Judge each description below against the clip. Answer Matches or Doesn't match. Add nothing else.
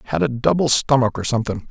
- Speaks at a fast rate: Matches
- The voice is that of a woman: Doesn't match